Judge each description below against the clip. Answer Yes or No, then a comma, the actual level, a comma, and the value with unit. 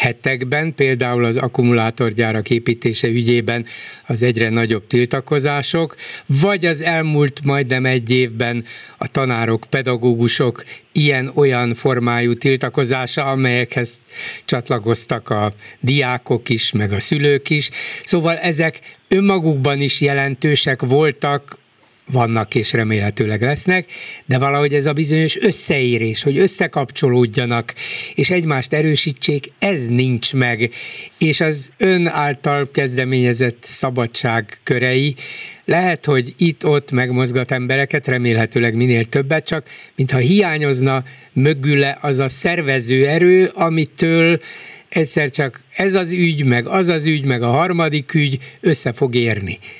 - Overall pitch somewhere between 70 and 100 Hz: No, low, 135 Hz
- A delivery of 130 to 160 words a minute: No, average, 115 wpm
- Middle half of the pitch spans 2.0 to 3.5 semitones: No, average, 3.9 semitones